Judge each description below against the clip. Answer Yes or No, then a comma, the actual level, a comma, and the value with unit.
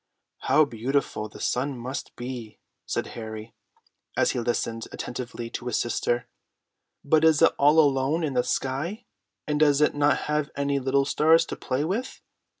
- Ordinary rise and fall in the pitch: Yes, average, 3.7 semitones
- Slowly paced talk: No, average, 160 wpm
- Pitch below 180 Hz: Yes, low, 135 Hz